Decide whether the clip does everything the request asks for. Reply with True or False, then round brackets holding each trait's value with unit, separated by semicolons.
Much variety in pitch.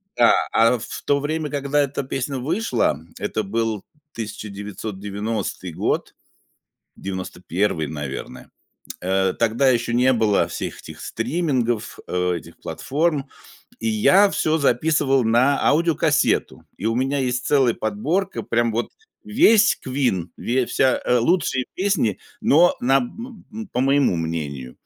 True (5.7 semitones)